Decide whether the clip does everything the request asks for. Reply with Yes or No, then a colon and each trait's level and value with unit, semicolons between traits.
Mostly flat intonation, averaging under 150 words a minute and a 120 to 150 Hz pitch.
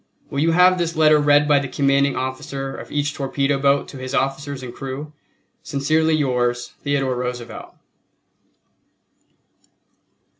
Yes: narrow, 2.1 semitones; slow, 135 wpm; medium, 140 Hz